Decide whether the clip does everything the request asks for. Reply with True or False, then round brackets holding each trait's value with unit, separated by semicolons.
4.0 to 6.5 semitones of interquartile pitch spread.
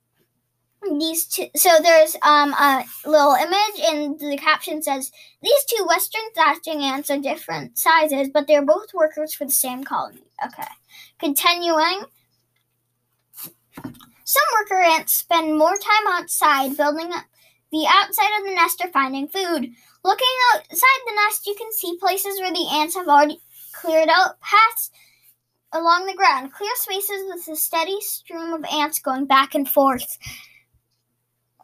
True (4.7 semitones)